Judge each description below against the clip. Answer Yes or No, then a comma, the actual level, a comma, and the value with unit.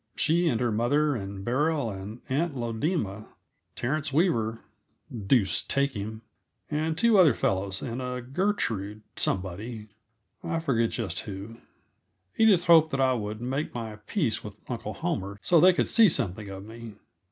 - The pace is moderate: Yes, average, 150 wpm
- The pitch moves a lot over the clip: Yes, wide, 6.5 semitones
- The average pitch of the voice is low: Yes, low, 120 Hz